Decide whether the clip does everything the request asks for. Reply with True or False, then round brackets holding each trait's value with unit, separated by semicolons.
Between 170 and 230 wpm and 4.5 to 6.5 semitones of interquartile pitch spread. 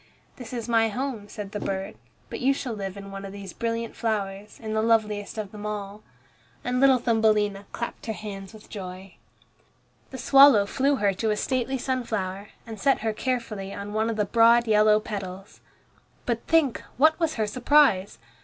False (185 wpm; 3.1 semitones)